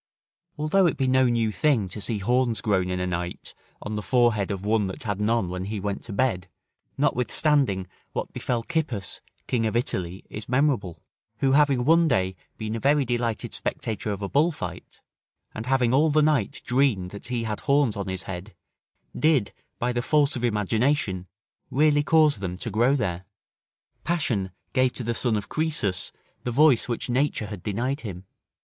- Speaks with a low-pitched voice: Yes, low, 115 Hz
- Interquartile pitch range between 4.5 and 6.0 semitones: Yes, wide, 5.5 semitones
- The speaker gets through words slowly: No, average, 180 wpm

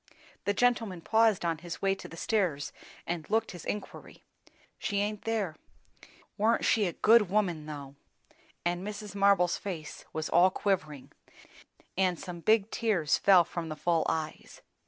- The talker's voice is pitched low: No, medium, 185 Hz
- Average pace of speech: Yes, average, 155 wpm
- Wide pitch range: No, average, 4.0 semitones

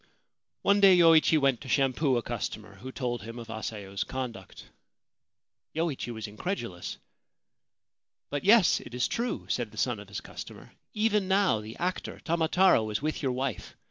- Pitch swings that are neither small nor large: No, wide, 7.4 semitones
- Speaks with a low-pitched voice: Yes, low, 130 Hz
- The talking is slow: No, average, 165 wpm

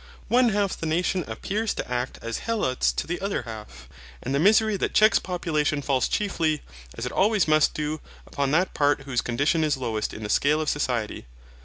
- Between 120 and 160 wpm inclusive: No, average, 195 wpm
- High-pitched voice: No, medium, 150 Hz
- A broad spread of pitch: Yes, wide, 6.7 semitones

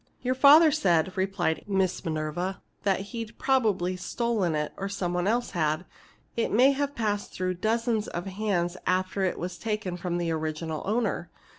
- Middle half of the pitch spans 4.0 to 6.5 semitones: Yes, average, 4.3 semitones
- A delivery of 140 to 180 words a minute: Yes, average, 160 wpm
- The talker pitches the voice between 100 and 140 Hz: No, high, 190 Hz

